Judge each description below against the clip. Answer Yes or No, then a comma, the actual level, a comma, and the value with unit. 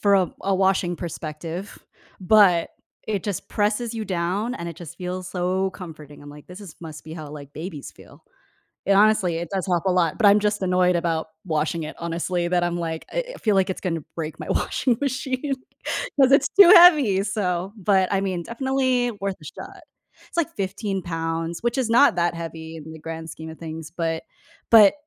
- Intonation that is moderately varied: Yes, average, 4.1 semitones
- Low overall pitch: No, medium, 180 Hz